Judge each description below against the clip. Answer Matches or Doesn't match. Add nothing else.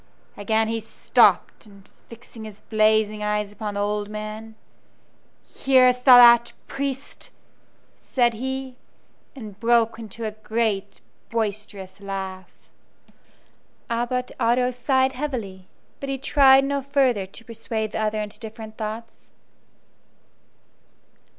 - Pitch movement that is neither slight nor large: Matches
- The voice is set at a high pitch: Matches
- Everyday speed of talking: Doesn't match